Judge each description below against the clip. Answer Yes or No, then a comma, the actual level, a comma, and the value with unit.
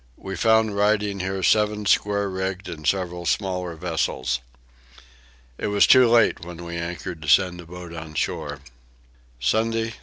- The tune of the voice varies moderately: Yes, average, 3.5 semitones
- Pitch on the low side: Yes, very low, 95 Hz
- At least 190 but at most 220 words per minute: No, average, 155 wpm